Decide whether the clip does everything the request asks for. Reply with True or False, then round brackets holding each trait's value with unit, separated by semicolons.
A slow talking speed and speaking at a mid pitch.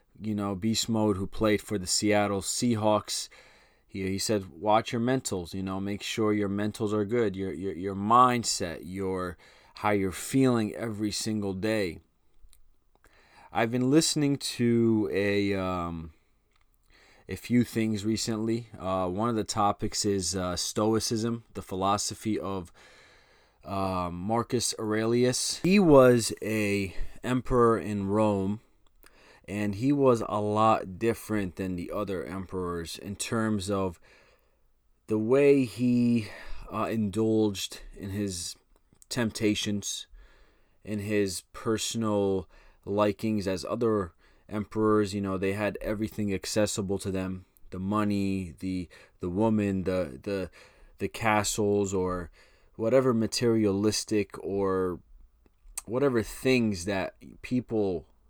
False (120 wpm; 105 Hz)